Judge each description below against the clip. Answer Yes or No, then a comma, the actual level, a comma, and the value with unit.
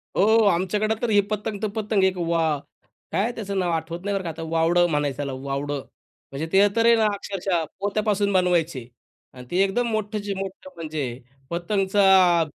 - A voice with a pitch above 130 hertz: Yes, high, 190 Hz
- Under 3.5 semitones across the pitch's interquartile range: No, average, 3.8 semitones